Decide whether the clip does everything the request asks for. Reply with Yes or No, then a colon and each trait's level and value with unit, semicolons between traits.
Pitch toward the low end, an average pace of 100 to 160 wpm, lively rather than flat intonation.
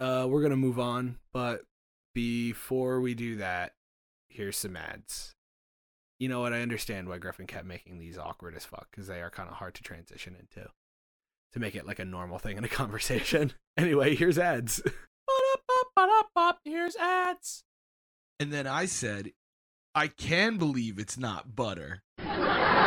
Yes: low, 120 Hz; average, 155 wpm; wide, 7.2 semitones